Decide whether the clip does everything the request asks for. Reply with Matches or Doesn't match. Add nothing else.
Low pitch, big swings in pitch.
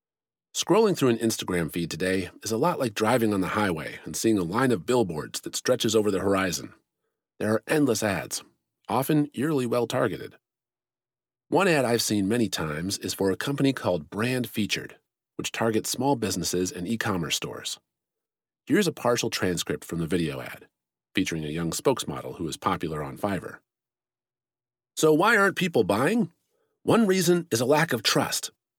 Matches